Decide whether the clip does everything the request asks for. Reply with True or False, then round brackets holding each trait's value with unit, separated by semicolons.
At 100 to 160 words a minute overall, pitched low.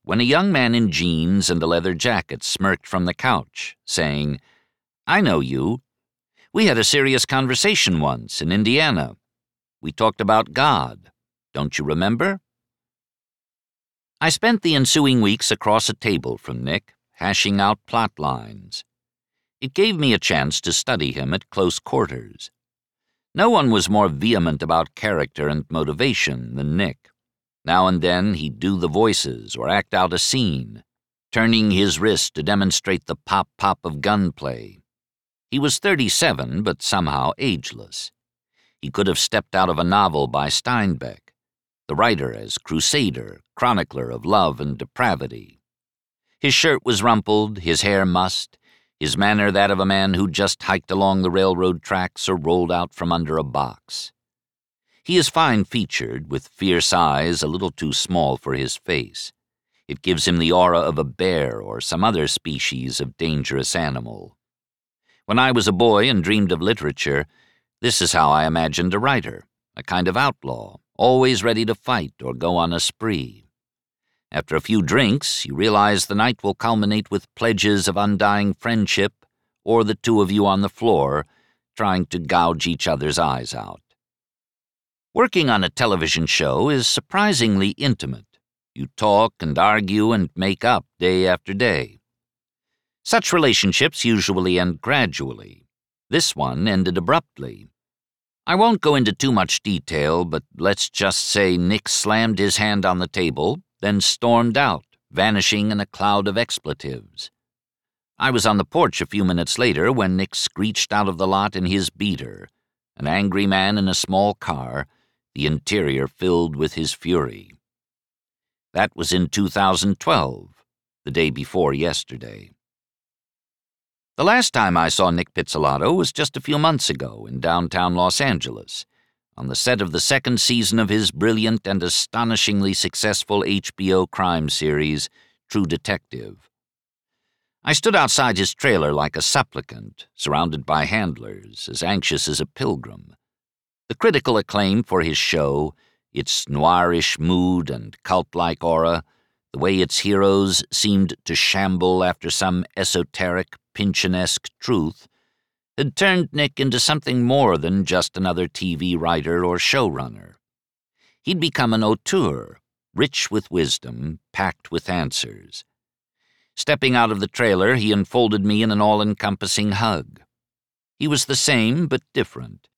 True (155 wpm; 95 Hz)